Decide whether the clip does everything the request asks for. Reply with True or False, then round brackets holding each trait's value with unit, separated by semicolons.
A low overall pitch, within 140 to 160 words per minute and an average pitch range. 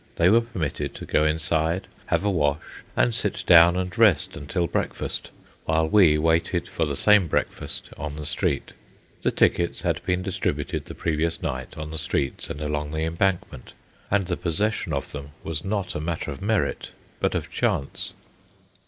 False (80 Hz; 175 wpm; 3.6 semitones)